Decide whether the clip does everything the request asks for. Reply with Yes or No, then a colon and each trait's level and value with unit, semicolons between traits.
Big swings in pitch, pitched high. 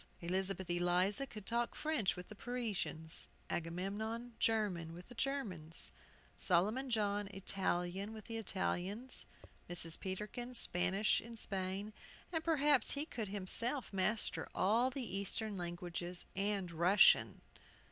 No: average, 4.3 semitones; high, 200 Hz